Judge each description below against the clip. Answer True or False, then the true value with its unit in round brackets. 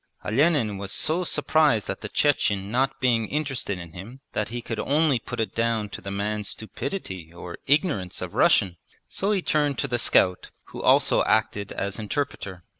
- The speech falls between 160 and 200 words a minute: True (180 wpm)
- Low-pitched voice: True (115 Hz)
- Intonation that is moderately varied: False (6.2 semitones)